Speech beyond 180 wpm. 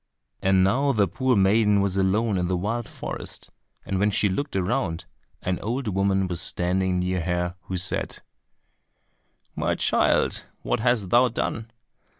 No: average, 150 wpm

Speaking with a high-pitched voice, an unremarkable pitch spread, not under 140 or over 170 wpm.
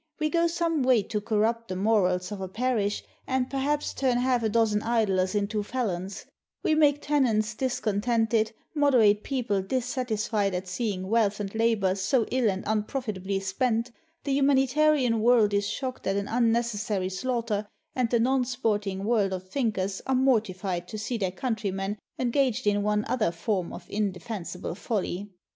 Yes: high, 220 Hz; average, 4.0 semitones; average, 165 wpm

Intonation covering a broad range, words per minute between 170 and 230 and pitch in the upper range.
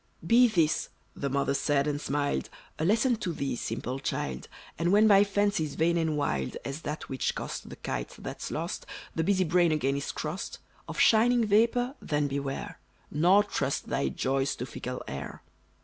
No: wide, 6.5 semitones; average, 175 wpm; medium, 155 Hz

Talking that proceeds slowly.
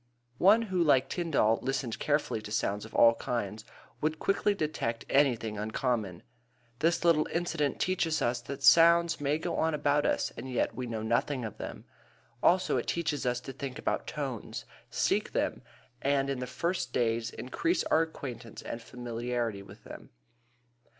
No: average, 165 wpm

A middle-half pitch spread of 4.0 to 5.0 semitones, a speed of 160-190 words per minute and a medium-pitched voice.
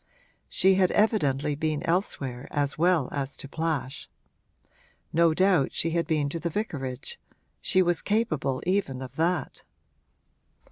No: average, 4.5 semitones; slow, 135 wpm; medium, 160 Hz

